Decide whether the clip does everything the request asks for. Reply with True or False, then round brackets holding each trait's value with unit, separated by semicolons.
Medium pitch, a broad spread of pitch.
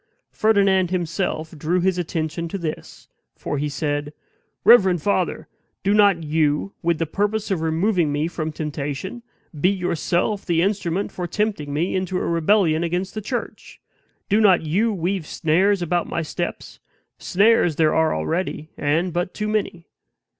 False (175 Hz; 3.9 semitones)